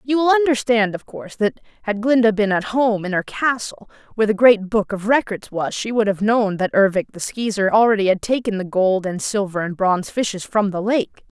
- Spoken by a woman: Yes, female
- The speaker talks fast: Yes, fast, 220 wpm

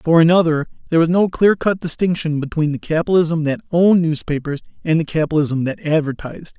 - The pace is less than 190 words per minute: Yes, average, 175 wpm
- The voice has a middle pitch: Yes, medium, 160 Hz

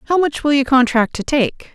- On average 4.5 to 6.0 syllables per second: Yes, 4.7 syllables/s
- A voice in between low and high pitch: No, very high, 265 Hz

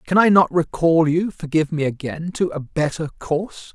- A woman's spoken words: No, male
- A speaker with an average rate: Yes, average, 160 wpm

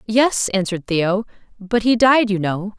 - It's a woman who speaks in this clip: Yes, female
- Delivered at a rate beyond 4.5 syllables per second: No, 4.4 syllables/s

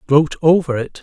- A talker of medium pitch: Yes, medium, 150 Hz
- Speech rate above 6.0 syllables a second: No, 4.8 syllables/s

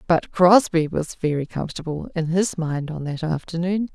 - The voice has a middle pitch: Yes, medium, 165 Hz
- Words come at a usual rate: Yes, average, 165 wpm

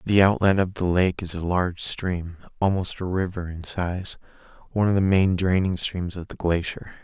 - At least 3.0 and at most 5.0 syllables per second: Yes, 4.9 syllables/s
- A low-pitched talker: Yes, very low, 90 Hz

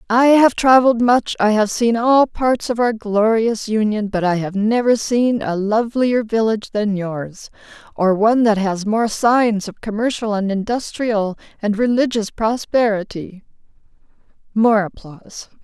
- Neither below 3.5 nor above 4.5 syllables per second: No, 4.8 syllables/s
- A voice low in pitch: No, high, 220 Hz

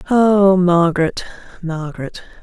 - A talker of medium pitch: Yes, medium, 180 Hz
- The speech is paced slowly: Yes, slow, 75 wpm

